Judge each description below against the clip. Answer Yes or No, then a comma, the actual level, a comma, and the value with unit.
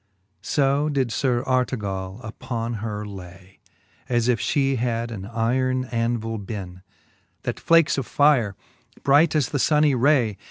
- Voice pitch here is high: No, low, 120 Hz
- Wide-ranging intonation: No, average, 4.2 semitones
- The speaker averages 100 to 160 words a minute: Yes, average, 145 wpm